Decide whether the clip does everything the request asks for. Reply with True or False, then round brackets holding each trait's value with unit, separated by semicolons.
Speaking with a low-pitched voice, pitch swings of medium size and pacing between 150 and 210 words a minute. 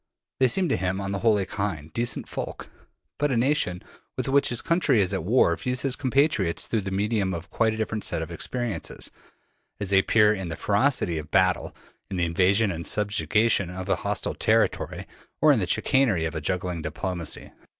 True (100 Hz; 4.6 semitones; 195 wpm)